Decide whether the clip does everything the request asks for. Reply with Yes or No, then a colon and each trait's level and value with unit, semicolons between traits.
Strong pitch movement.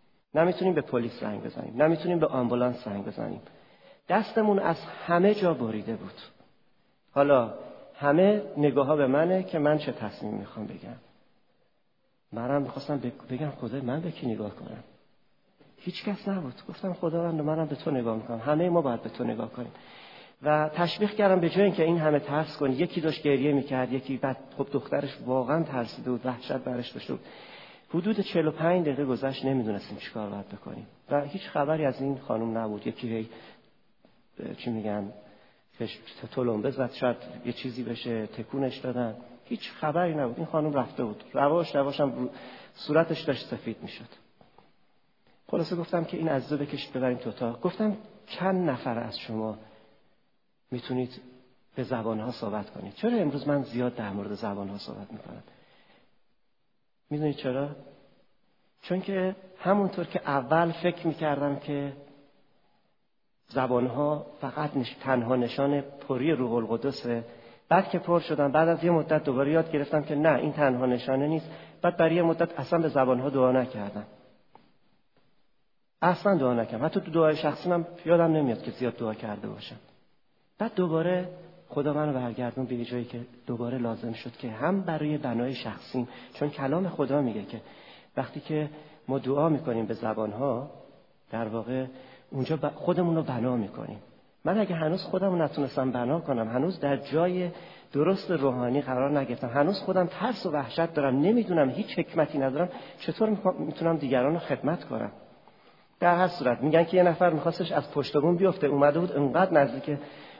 No: average, 5.0 semitones